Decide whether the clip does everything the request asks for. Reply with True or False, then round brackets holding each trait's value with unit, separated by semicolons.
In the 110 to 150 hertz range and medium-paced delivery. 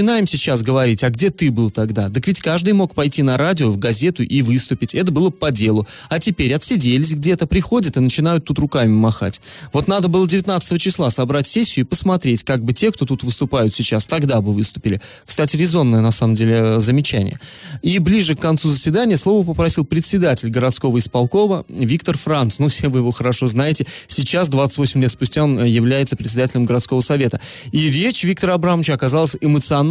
False (140 Hz; 185 wpm)